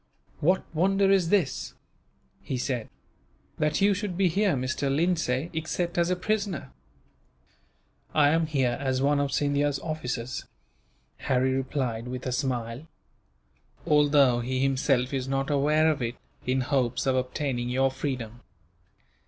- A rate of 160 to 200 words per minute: No, slow, 135 wpm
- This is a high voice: No, medium, 140 Hz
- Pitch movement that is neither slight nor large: Yes, average, 3.7 semitones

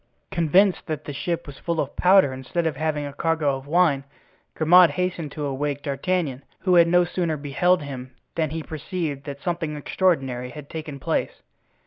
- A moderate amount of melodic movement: Yes, average, 3.6 semitones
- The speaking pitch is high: No, medium, 155 Hz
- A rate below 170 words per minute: No, average, 175 wpm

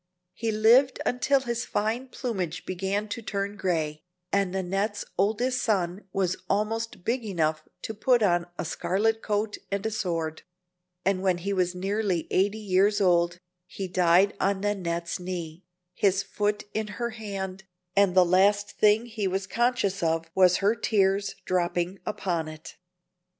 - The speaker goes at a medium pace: Yes, average, 150 wpm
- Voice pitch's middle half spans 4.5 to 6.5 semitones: No, average, 3.0 semitones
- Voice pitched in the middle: No, high, 195 Hz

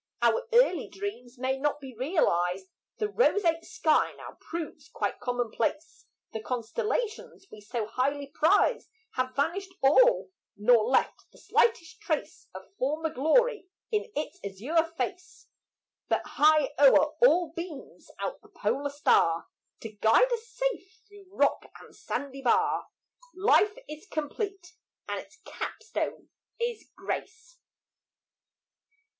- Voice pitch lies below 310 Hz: No, very high, 315 Hz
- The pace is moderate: No, slow, 125 wpm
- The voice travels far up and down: Yes, wide, 7.9 semitones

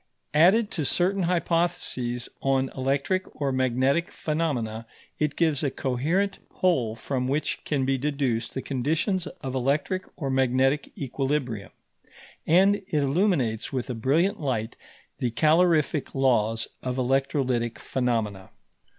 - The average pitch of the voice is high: No, low, 135 Hz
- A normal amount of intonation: Yes, average, 4.5 semitones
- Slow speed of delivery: Yes, slow, 125 wpm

